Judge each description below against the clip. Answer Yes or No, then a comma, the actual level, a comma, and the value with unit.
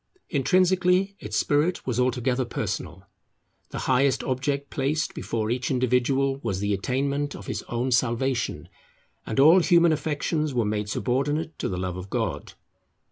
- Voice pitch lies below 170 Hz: Yes, low, 135 Hz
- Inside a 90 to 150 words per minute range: Yes, average, 145 wpm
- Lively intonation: No, average, 4.0 semitones